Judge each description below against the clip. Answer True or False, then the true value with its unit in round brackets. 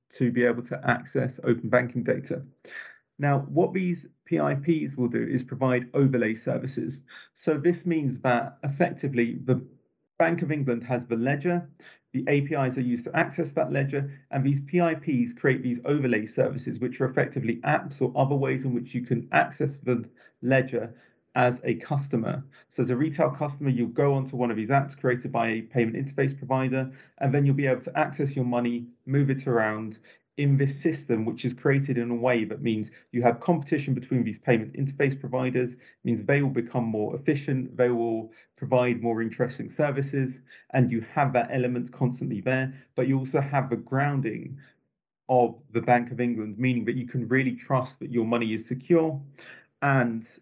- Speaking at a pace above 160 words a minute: True (180 wpm)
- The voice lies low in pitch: True (130 Hz)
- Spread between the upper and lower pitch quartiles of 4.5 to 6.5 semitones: False (2.6 semitones)